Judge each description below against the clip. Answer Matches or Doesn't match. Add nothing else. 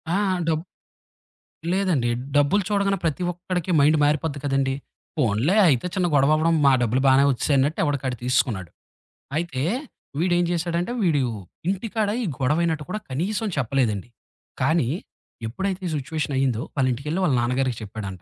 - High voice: Doesn't match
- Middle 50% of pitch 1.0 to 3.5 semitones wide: Doesn't match